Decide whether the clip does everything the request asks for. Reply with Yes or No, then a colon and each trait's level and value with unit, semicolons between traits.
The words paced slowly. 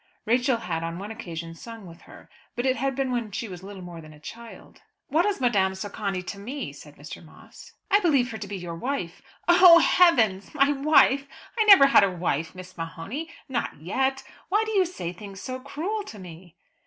No: fast, 205 wpm